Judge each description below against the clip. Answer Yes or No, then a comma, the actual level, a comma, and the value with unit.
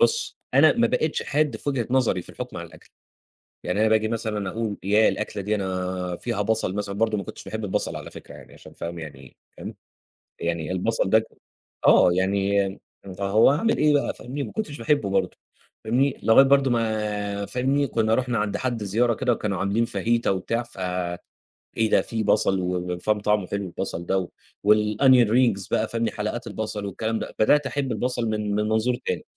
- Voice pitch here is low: Yes, low, 110 Hz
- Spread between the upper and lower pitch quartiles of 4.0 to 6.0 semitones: No, average, 3.3 semitones